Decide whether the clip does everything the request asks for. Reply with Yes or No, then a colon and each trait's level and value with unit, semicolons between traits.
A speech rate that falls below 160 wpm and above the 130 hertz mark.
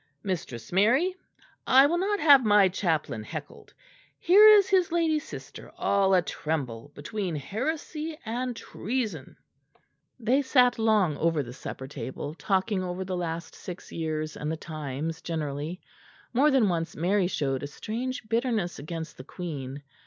Yes: average, 145 wpm; medium, 185 Hz